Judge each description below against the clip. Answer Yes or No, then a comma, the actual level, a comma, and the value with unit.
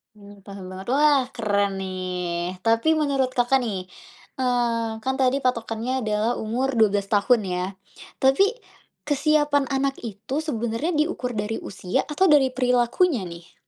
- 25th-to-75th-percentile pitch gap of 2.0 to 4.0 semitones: No, average, 4.9 semitones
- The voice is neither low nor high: No, high, 235 Hz